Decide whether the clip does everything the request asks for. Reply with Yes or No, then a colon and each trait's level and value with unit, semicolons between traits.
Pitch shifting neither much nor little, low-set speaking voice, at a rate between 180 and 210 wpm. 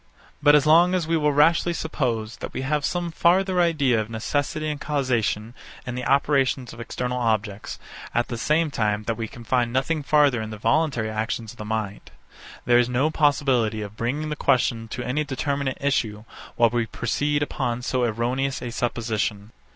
Yes: average, 4.6 semitones; low, 125 Hz; average, 185 wpm